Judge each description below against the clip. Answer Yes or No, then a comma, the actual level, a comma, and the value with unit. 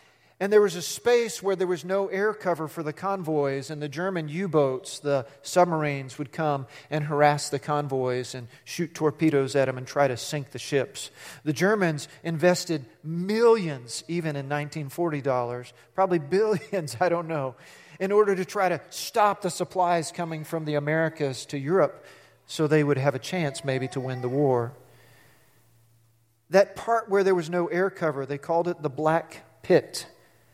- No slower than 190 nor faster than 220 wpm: No, average, 175 wpm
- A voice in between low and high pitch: Yes, medium, 155 Hz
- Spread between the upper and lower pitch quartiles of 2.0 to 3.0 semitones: No, average, 4.5 semitones